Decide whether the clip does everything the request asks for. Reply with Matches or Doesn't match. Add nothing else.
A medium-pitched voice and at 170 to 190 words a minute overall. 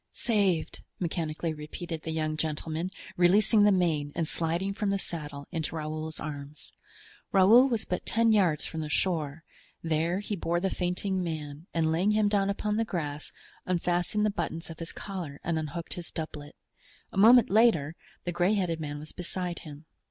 Matches